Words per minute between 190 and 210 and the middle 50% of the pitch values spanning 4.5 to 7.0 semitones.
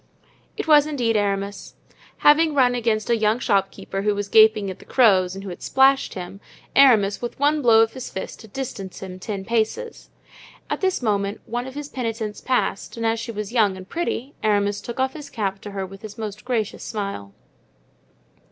No: average, 195 wpm; average, 4.1 semitones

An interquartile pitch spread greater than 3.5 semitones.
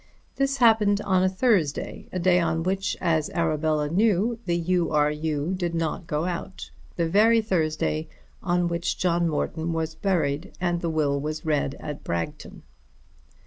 No: average, 3.1 semitones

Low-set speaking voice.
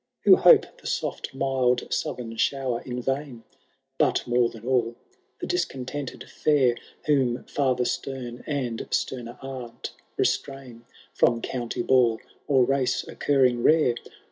Yes: low, 125 Hz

